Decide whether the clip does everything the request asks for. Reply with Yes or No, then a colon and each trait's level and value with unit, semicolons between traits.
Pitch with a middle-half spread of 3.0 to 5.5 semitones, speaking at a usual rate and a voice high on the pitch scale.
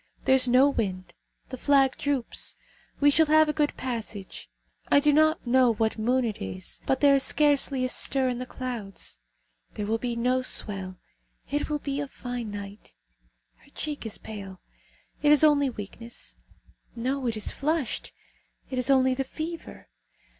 Yes: average, 4.3 semitones; average, 170 wpm; very high, 255 Hz